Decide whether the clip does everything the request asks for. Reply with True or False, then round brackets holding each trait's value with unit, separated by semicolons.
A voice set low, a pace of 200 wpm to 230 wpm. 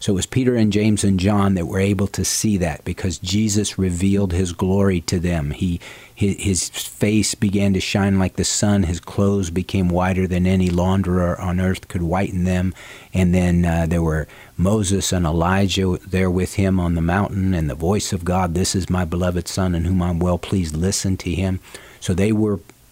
True (95 Hz; 205 wpm)